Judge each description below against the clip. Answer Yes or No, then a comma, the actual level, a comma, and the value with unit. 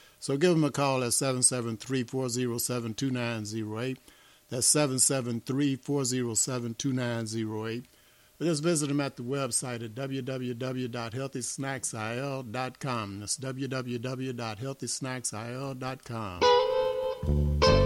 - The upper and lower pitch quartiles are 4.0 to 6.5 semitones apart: No, narrow, 2.5 semitones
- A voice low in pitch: Yes, low, 130 Hz